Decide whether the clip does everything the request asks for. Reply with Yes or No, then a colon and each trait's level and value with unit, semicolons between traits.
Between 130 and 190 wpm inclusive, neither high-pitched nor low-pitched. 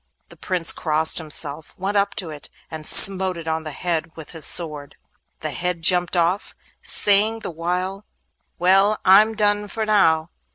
Yes: average, 165 wpm; medium, 180 Hz